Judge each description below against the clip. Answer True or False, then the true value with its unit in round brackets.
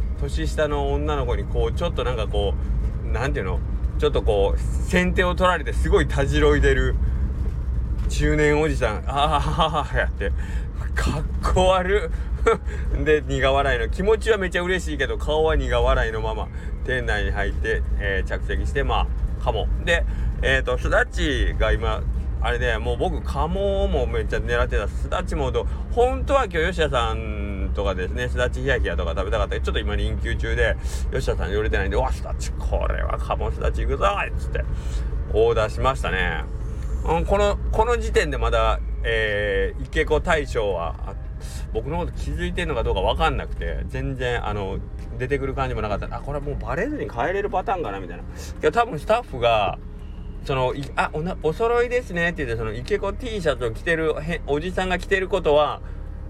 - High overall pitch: False (95 Hz)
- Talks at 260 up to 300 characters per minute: False (365 characters per minute)